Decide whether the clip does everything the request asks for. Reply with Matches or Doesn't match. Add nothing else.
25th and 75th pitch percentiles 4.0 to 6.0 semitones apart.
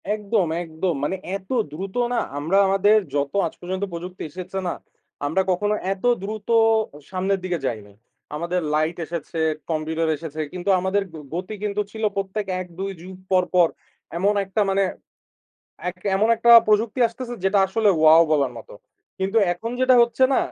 Doesn't match